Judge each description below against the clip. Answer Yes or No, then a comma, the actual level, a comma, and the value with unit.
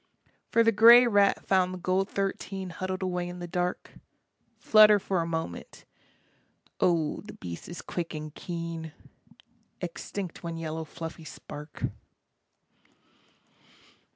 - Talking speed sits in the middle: No, slow, 125 wpm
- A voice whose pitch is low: No, medium, 180 Hz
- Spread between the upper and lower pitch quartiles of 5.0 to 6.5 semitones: No, average, 2.9 semitones